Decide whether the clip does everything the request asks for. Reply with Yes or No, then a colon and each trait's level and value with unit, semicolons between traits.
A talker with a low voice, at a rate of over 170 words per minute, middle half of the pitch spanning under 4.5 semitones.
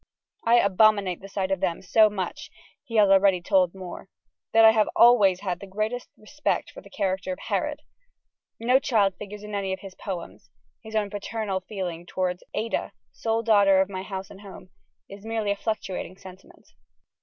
No: high, 200 Hz; average, 180 wpm; narrow, 2.5 semitones